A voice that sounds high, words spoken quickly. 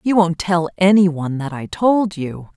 No: medium, 175 Hz; fast, 210 wpm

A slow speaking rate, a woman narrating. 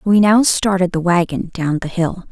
No: fast, 205 wpm; female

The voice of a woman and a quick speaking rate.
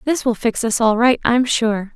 Yes: female; fast, 245 wpm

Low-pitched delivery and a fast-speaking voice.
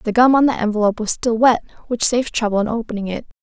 No: high, 225 Hz; fast, 245 wpm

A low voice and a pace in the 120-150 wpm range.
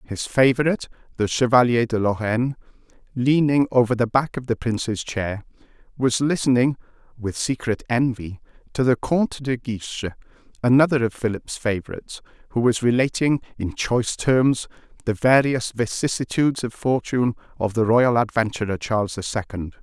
Yes: low, 120 Hz; average, 140 wpm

